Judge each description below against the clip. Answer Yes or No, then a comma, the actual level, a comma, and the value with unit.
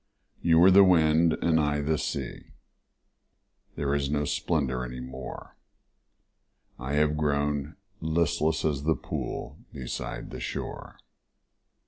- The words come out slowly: Yes, slow, 120 wpm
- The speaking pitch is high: No, very low, 75 Hz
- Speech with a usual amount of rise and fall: No, narrow, 2.3 semitones